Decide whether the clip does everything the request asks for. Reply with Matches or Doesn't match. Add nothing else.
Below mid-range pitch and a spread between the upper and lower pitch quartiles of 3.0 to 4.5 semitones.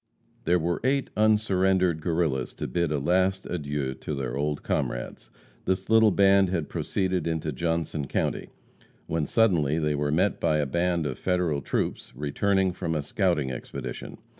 Matches